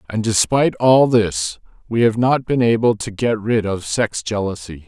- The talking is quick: No, average, 185 wpm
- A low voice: Yes, low, 110 Hz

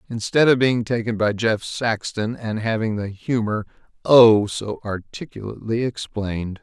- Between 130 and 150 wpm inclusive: Yes, slow, 135 wpm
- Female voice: No, male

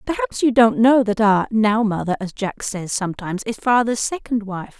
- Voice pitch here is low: No, high, 220 Hz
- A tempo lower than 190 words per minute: No, average, 200 wpm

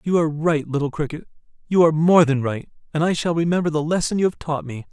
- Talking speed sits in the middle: No, fast, 245 wpm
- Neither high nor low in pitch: Yes, medium, 155 Hz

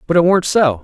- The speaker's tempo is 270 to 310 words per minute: Yes, fast, 290 wpm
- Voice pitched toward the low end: No, medium, 160 Hz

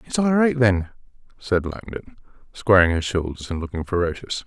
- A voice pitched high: No, low, 105 Hz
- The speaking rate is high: No, average, 160 wpm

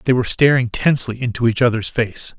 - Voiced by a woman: No, male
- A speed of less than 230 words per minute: Yes, average, 200 wpm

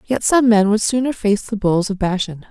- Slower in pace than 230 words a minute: No, fast, 240 wpm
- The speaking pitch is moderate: No, high, 210 Hz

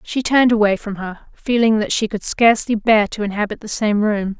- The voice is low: No, high, 215 Hz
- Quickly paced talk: Yes, fast, 220 wpm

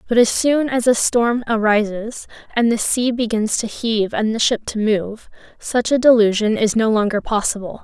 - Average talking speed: Yes, average, 190 wpm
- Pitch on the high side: Yes, high, 225 Hz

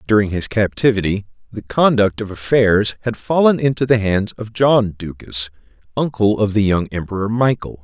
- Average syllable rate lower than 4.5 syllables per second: No, 5.0 syllables/s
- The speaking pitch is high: No, low, 110 Hz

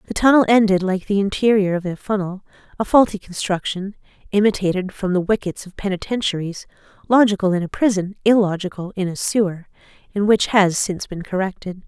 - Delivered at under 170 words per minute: Yes, average, 160 wpm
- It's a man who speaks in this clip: No, female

